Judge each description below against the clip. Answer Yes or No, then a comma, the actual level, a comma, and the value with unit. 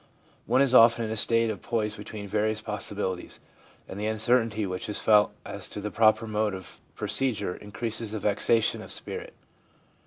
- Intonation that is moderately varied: No, narrow, 1.7 semitones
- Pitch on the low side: Yes, low, 110 Hz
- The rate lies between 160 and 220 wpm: Yes, average, 175 wpm